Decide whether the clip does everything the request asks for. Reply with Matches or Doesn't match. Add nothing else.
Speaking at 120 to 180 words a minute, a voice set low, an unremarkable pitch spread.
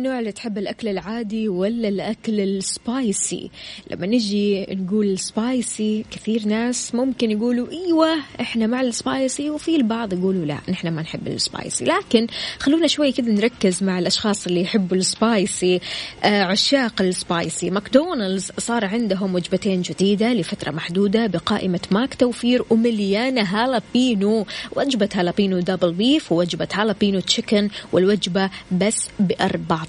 Doesn't match